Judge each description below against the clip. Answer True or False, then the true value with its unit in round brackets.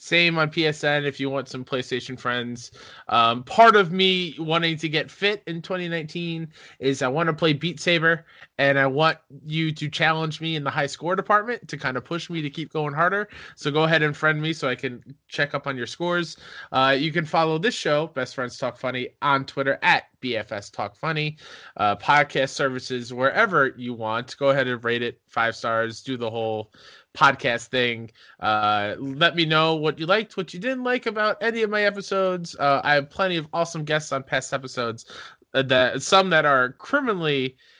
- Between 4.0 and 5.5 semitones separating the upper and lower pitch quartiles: True (4.4 semitones)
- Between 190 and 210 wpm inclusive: True (200 wpm)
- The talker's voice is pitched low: False (150 Hz)